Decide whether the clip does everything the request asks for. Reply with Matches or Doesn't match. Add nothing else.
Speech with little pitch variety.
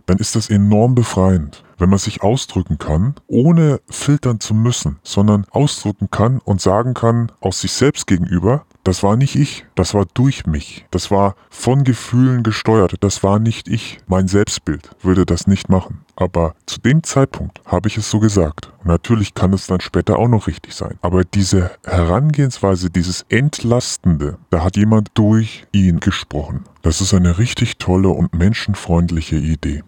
Doesn't match